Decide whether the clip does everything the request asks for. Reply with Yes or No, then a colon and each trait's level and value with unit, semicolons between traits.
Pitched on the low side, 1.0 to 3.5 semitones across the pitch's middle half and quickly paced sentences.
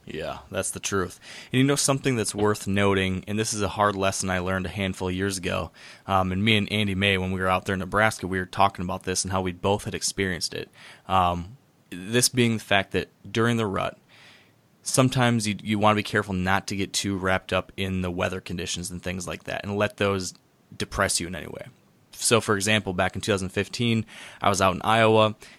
Yes: low, 100 Hz; narrow, 2.5 semitones; fast, 235 wpm